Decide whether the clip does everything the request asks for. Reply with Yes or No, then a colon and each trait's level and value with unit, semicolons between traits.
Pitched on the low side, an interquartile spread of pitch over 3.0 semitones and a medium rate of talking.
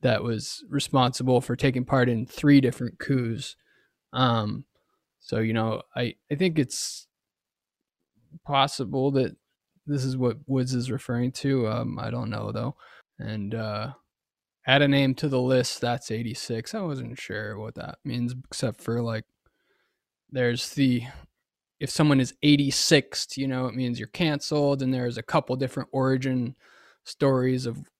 No: low, 130 Hz; average, 2.7 semitones; average, 150 wpm